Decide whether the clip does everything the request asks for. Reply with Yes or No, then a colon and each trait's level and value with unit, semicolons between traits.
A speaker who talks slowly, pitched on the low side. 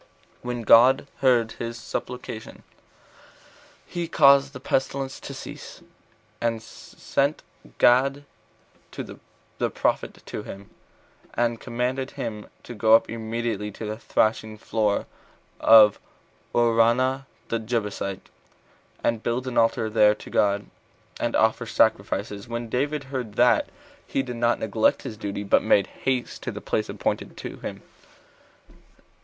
Yes: slow, 125 wpm; low, 115 Hz